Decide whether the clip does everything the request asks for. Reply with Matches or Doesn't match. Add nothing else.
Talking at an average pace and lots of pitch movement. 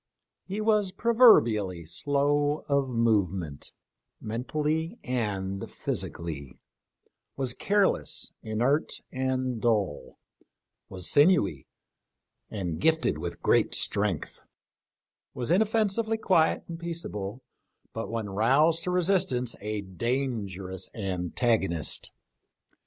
Doesn't match